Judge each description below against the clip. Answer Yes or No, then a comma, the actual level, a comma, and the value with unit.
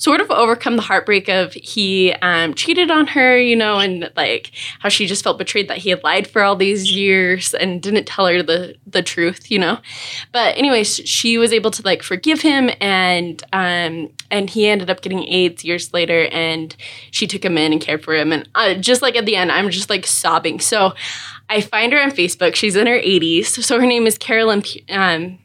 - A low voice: No, high, 195 Hz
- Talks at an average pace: No, fast, 215 wpm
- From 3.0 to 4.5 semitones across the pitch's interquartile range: Yes, average, 4.1 semitones